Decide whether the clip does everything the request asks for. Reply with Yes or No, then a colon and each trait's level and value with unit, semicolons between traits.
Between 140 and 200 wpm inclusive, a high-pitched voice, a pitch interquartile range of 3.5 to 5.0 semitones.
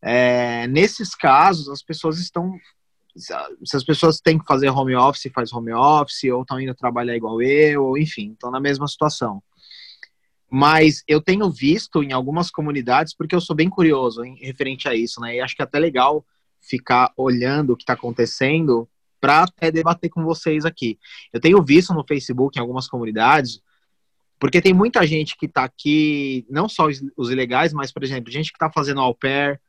No: fast, 185 wpm; medium, 140 Hz; average, 4.0 semitones